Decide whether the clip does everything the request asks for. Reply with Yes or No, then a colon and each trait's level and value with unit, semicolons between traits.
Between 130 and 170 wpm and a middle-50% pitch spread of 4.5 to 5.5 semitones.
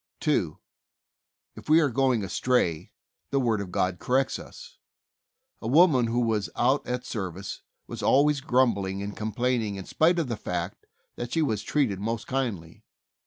Yes: average, 165 wpm; average, 5.1 semitones